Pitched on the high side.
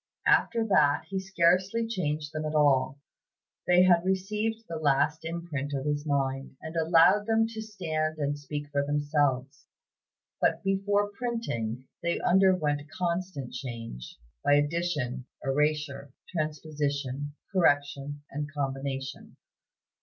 No: medium, 150 Hz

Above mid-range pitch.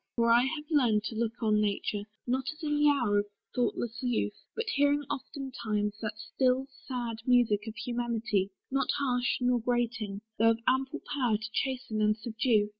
Yes: high, 240 Hz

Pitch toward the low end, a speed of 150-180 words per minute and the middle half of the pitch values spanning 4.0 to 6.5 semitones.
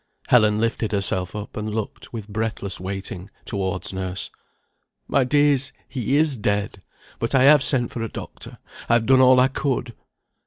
Yes: low, 115 Hz; average, 165 wpm; average, 4.4 semitones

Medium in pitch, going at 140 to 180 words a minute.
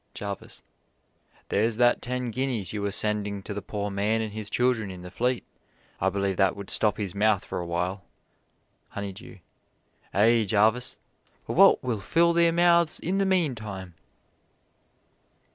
No: low, 105 Hz; average, 155 wpm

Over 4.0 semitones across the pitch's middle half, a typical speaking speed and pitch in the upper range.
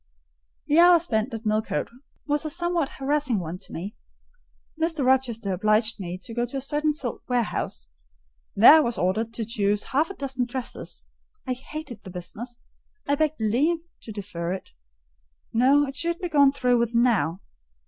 Yes: average, 5.3 semitones; average, 170 wpm; high, 245 Hz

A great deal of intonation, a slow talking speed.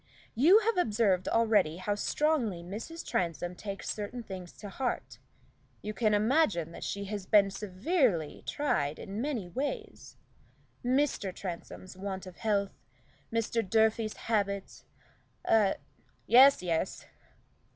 No: average, 4.2 semitones; slow, 125 wpm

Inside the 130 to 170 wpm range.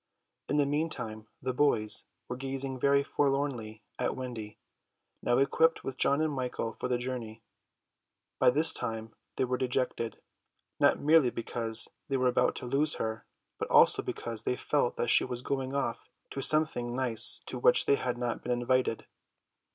Yes: average, 165 wpm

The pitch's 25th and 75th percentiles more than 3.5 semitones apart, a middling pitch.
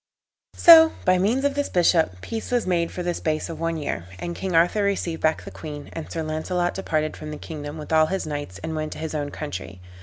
No: average, 3.0 semitones; medium, 160 Hz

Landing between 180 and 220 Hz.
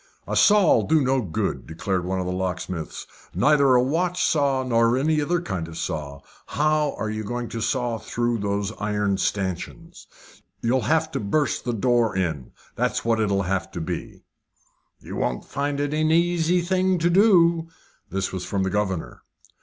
No: low, 120 Hz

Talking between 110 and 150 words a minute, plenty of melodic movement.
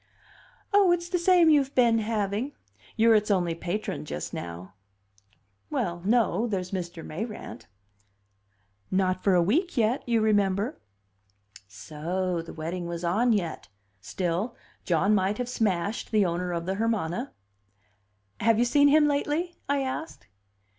Yes: average, 140 wpm; wide, 5.8 semitones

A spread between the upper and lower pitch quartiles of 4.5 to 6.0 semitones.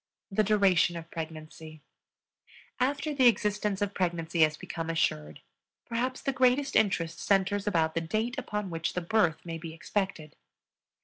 Yes: average, 4.8 semitones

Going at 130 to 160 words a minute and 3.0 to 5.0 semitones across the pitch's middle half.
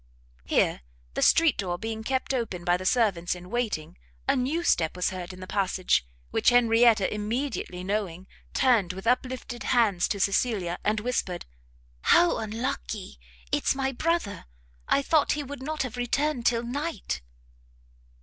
No: average, 150 wpm; wide, 5.6 semitones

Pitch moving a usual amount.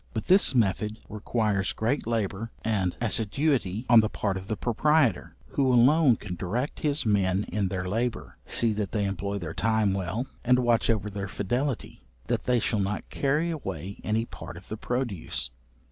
Yes: average, 3.9 semitones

